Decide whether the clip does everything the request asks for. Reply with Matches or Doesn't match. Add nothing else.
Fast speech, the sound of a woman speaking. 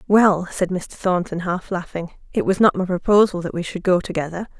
Matches